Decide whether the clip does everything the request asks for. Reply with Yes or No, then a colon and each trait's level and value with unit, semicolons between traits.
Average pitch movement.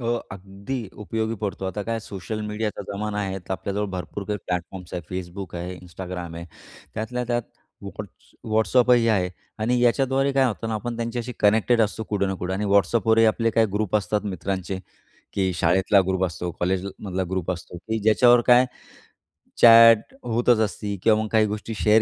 Yes: average, 3.3 semitones